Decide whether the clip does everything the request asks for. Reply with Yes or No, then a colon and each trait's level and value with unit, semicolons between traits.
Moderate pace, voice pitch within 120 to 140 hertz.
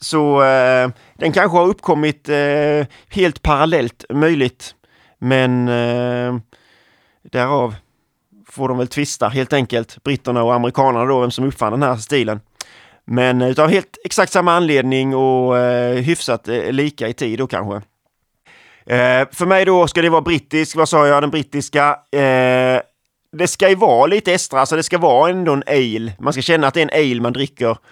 Yes: average, 175 wpm; low, 135 Hz